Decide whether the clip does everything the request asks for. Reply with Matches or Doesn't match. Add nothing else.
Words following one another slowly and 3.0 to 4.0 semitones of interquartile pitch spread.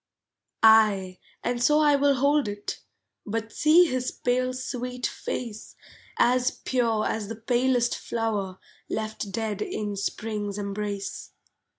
Matches